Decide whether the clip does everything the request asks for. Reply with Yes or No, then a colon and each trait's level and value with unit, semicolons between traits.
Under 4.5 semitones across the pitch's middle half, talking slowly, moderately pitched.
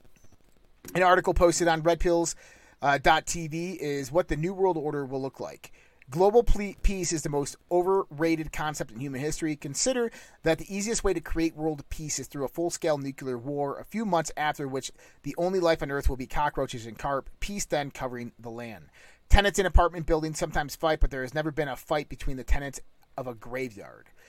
No: average, 4.1 semitones; average, 200 wpm; medium, 155 Hz